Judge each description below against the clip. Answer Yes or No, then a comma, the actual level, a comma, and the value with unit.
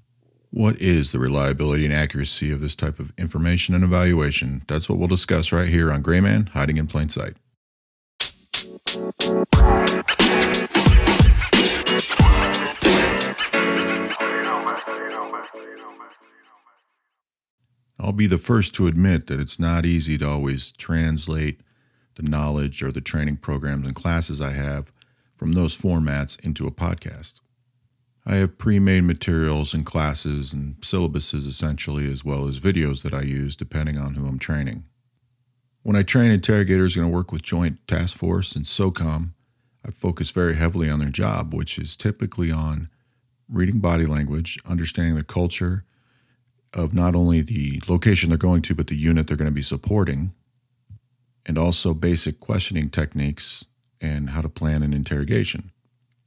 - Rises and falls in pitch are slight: No, average, 5.3 semitones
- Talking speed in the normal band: Yes, average, 145 wpm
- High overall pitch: No, very low, 85 Hz